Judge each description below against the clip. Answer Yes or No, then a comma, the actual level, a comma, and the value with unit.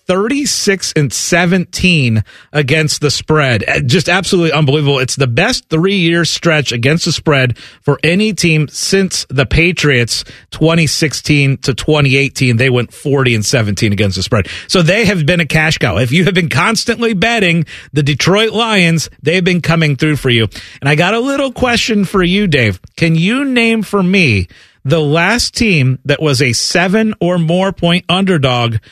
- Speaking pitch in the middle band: Yes, medium, 160 Hz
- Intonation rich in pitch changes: Yes, wide, 5.7 semitones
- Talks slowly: No, average, 170 wpm